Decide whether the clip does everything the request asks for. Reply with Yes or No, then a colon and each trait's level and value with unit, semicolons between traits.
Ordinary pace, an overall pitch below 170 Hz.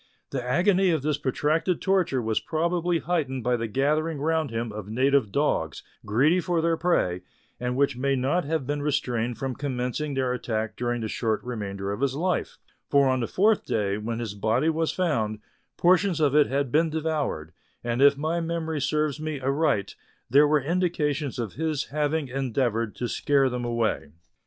Yes: average, 180 wpm; medium, 140 Hz